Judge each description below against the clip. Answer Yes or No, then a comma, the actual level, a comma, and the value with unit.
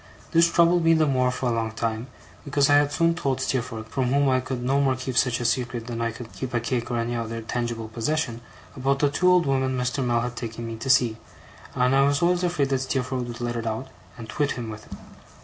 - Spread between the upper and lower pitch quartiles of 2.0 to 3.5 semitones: Yes, average, 2.9 semitones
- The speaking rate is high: Yes, fast, 250 wpm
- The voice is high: No, low, 125 Hz